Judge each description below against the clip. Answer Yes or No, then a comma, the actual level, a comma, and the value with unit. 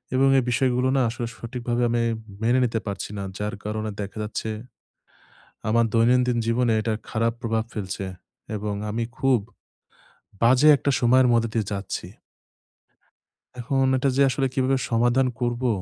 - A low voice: Yes, low, 120 Hz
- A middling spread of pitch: No, narrow, 2.3 semitones